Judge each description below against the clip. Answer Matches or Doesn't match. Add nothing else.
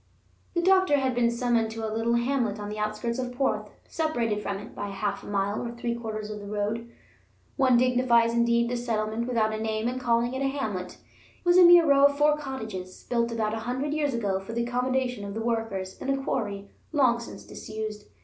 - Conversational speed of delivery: Doesn't match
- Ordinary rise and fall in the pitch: Matches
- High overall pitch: Matches